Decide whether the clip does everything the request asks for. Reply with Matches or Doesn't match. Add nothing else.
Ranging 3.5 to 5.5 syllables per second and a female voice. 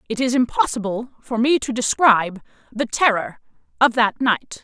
Matches